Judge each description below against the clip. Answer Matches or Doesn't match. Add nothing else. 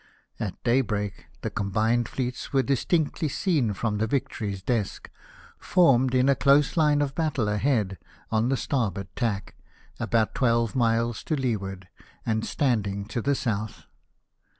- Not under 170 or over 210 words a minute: Doesn't match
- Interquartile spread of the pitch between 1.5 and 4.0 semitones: Doesn't match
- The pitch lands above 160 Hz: Doesn't match